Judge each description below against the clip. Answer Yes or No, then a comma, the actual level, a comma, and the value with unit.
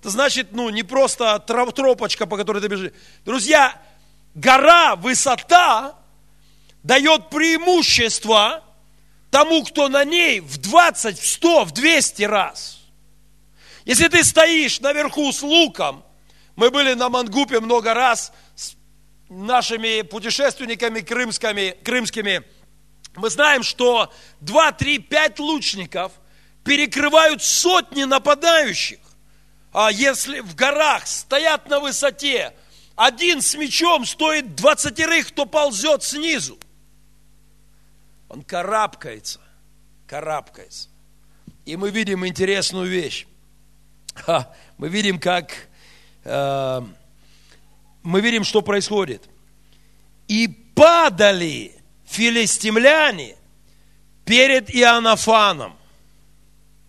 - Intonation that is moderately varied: No, wide, 6.0 semitones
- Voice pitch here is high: Yes, high, 245 Hz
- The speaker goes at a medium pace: No, slow, 90 wpm